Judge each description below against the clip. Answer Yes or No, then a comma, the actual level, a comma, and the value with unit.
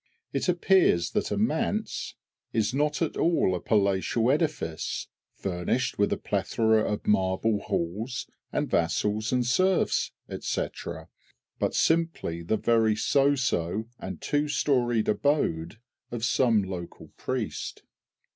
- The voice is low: Yes, low, 110 Hz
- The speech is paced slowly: Yes, slow, 125 wpm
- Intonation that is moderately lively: No, wide, 6.3 semitones